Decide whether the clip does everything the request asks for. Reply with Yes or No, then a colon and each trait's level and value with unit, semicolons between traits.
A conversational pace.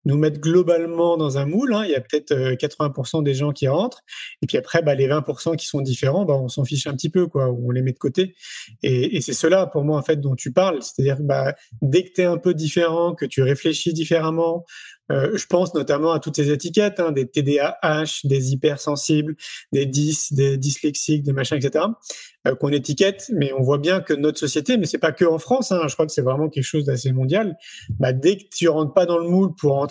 No: fast, 250 wpm